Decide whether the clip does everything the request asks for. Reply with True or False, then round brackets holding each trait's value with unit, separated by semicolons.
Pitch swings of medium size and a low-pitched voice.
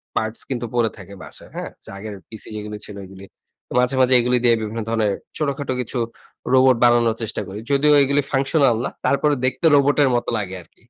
True (4.0 semitones; 120 Hz)